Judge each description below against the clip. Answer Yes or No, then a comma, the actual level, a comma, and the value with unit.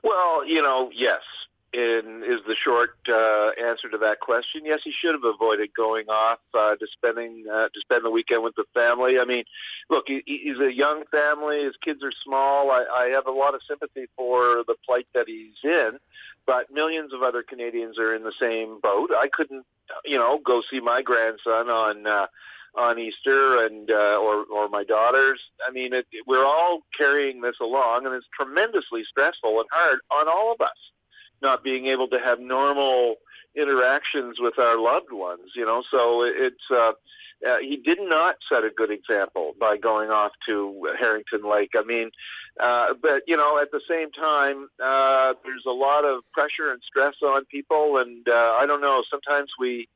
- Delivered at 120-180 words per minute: No, average, 195 wpm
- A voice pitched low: Yes, low, 125 Hz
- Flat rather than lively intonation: No, average, 4.1 semitones